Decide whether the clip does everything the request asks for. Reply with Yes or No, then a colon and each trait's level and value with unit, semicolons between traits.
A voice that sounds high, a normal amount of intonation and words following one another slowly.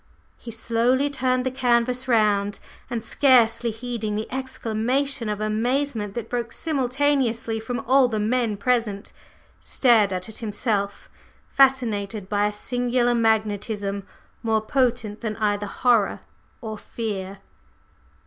Yes: high, 230 Hz; average, 3.0 semitones; slow, 120 wpm